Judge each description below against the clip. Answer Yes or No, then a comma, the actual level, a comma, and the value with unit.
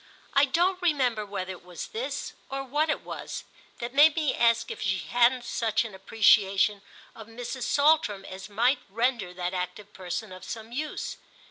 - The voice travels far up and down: Yes, wide, 5.8 semitones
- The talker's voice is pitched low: No, high, 230 Hz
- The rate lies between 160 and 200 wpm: Yes, average, 170 wpm